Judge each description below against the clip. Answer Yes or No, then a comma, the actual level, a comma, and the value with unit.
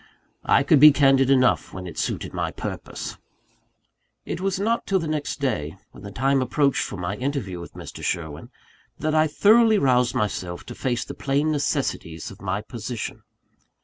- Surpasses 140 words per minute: Yes, average, 175 wpm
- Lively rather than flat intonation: Yes, wide, 7.2 semitones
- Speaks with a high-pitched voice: No, low, 135 Hz